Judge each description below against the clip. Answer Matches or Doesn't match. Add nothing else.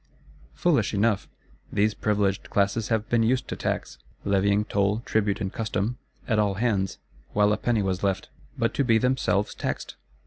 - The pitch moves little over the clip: Matches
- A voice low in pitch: Matches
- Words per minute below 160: Doesn't match